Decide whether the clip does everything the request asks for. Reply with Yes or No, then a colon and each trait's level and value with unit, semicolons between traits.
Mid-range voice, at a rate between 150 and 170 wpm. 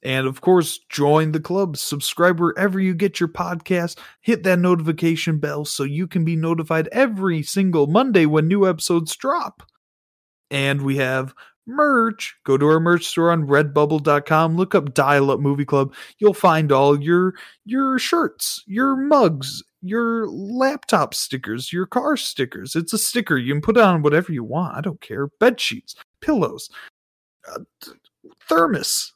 Yes: medium, 170 Hz; average, 160 wpm